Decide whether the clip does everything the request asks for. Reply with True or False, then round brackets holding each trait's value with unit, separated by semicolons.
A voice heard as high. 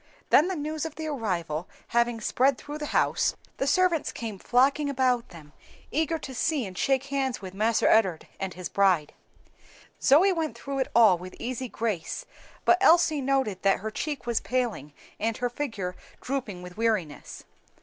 True (245 Hz)